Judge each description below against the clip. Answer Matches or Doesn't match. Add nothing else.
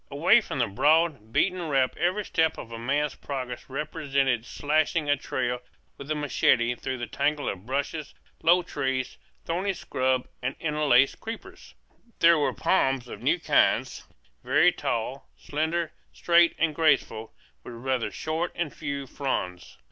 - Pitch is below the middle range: Doesn't match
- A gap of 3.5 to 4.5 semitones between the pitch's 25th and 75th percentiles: Matches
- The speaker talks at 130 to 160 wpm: Matches